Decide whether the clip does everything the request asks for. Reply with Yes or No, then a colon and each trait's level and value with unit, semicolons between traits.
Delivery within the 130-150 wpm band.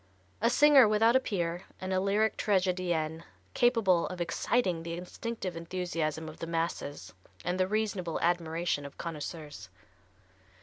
Yes: slow, 135 wpm